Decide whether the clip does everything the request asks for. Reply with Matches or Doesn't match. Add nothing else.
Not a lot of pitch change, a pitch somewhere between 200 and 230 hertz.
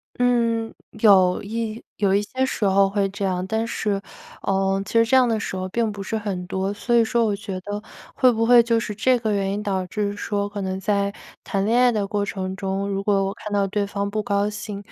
Matches